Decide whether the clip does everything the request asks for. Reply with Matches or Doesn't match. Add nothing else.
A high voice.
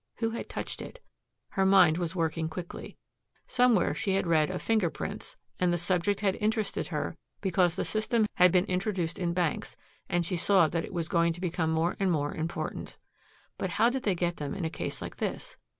Doesn't match